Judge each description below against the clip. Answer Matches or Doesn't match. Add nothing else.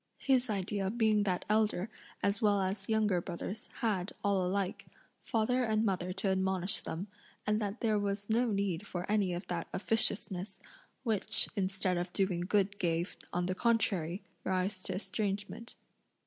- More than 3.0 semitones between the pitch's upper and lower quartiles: Doesn't match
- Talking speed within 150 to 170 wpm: Matches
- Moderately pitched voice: Doesn't match